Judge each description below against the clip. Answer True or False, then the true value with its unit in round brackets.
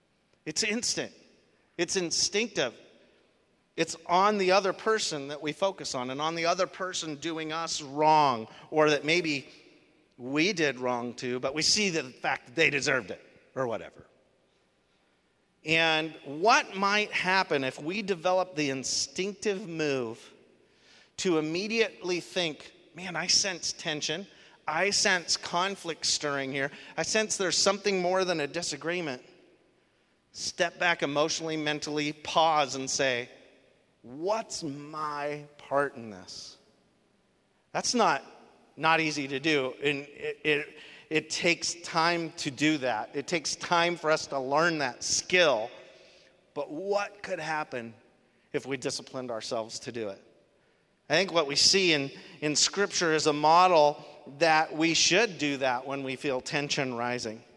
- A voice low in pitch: False (155 Hz)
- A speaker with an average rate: True (145 wpm)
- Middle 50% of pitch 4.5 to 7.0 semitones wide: False (3.8 semitones)